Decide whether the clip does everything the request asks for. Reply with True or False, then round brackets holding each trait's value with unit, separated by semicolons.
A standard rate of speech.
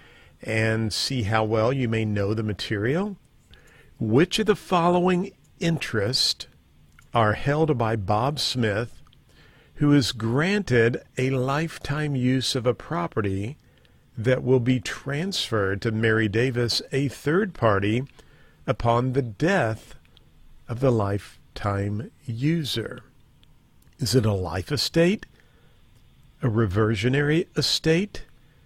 False (110 wpm)